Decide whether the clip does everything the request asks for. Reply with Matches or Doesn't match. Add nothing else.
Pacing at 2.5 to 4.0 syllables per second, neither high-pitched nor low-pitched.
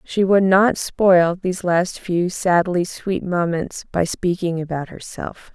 Matches